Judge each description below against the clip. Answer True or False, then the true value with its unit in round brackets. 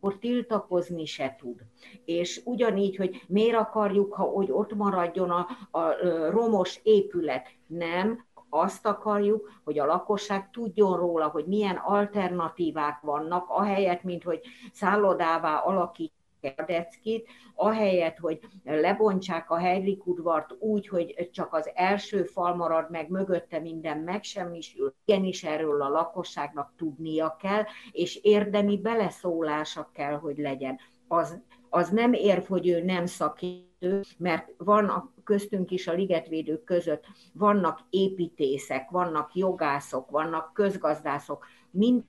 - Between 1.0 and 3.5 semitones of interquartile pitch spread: False (4.2 semitones)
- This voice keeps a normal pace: True (125 wpm)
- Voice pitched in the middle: True (180 Hz)